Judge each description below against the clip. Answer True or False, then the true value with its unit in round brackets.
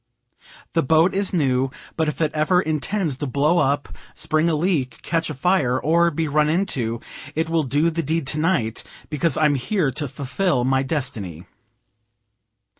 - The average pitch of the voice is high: False (155 Hz)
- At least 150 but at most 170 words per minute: True (160 wpm)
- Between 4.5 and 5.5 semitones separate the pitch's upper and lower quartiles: False (3.8 semitones)